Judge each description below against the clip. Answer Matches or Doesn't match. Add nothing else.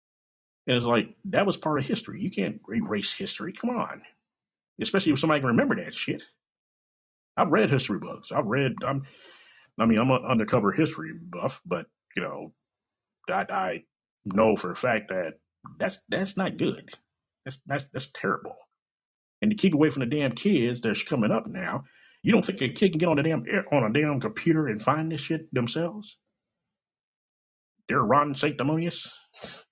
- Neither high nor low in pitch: Matches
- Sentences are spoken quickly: Doesn't match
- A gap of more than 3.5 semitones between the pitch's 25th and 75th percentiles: Matches